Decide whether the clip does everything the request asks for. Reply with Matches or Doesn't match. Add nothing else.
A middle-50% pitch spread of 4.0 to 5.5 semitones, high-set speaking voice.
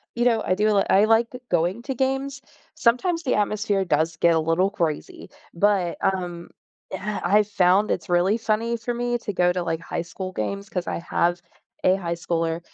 Matches